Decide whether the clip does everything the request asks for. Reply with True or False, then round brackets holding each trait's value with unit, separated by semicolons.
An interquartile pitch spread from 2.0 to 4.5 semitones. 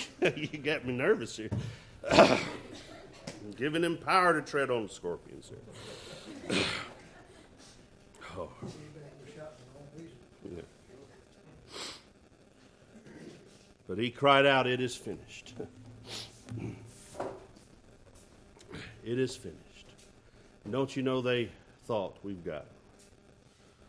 False (4.9 semitones)